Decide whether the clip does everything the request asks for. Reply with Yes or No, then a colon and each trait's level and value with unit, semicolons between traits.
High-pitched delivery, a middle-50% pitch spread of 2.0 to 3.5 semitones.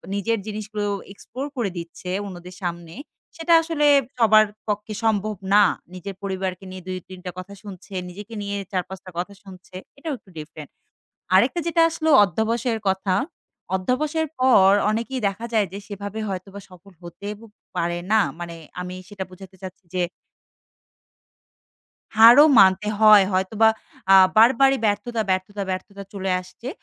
Yes: high, 200 Hz; average, 3.1 semitones